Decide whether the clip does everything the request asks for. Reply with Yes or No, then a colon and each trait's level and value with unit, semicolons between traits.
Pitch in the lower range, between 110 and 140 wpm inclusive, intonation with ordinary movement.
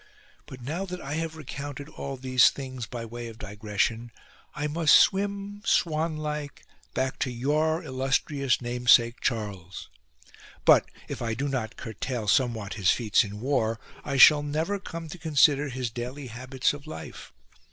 No: low, 130 Hz; average, 155 wpm; average, 4.3 semitones